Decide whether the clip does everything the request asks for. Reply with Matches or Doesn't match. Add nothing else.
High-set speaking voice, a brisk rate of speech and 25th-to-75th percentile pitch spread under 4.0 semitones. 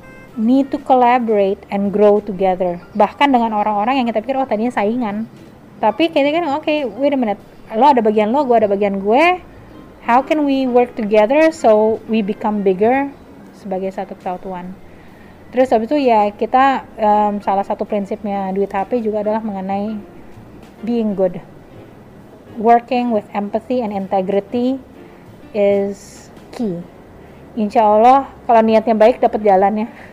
Matches